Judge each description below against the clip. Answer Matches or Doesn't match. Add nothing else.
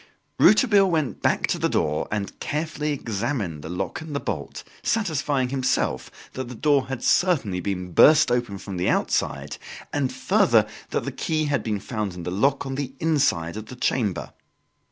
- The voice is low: Matches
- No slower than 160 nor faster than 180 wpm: Matches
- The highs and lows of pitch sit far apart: Matches